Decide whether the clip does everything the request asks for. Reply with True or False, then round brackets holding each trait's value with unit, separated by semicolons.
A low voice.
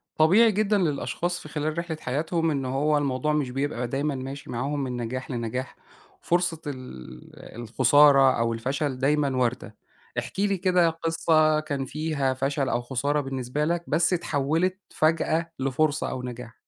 False (145 Hz)